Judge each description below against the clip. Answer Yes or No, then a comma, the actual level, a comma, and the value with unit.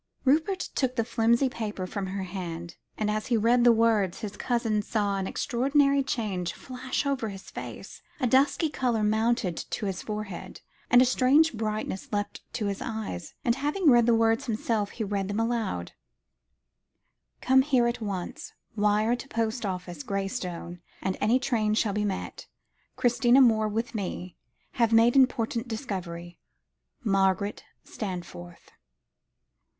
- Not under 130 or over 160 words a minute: Yes, average, 150 wpm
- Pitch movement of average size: Yes, average, 3.7 semitones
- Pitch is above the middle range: Yes, high, 220 Hz